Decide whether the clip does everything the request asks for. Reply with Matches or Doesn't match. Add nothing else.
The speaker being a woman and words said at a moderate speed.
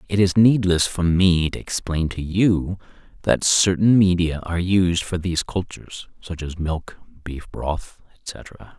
Doesn't match